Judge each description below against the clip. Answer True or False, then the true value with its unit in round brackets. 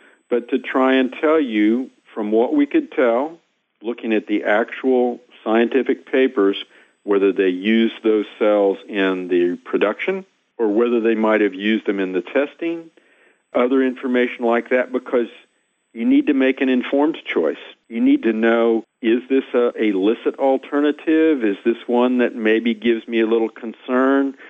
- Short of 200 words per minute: True (160 wpm)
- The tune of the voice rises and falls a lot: False (3.5 semitones)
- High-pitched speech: False (120 Hz)